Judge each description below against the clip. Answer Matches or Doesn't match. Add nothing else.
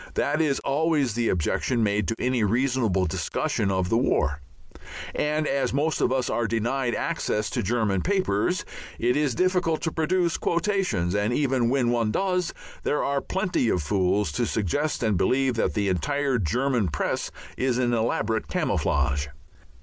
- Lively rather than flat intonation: Matches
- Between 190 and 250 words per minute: Doesn't match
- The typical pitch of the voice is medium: Doesn't match